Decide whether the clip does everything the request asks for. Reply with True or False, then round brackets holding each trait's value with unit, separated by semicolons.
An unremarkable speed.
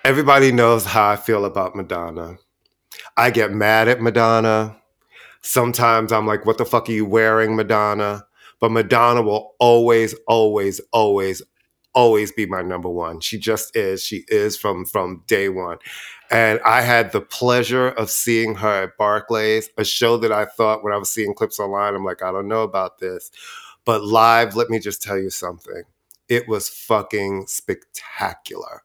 True (170 wpm)